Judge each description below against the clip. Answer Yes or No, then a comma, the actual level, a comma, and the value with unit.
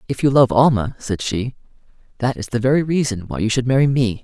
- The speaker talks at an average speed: No, fast, 225 wpm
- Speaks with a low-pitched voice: Yes, low, 120 Hz